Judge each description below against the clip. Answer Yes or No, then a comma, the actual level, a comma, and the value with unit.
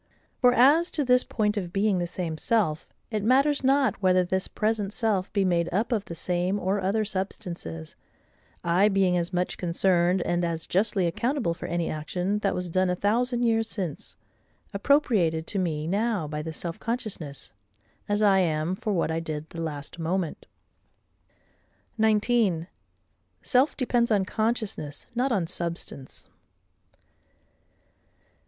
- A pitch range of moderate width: Yes, average, 4.5 semitones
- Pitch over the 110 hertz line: Yes, high, 190 Hz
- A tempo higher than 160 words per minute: No, average, 150 wpm